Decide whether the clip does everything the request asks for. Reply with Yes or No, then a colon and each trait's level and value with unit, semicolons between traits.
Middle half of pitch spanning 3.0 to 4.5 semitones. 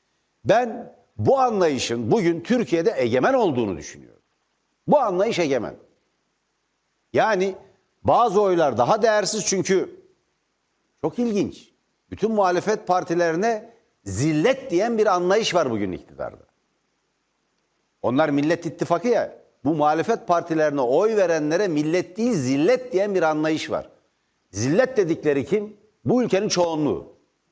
No: average, 5.1 semitones